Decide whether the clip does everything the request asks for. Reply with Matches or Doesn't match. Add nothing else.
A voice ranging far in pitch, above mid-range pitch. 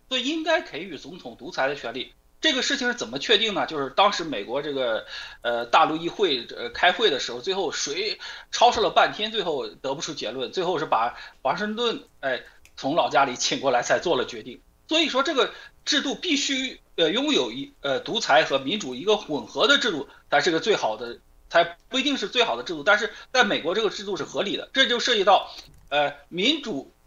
Matches